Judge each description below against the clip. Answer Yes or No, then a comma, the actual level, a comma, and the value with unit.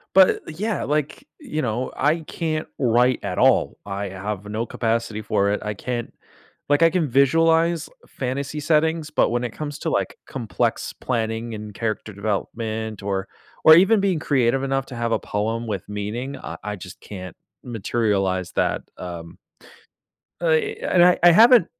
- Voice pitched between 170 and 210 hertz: No, low, 120 Hz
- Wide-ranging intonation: Yes, wide, 6.7 semitones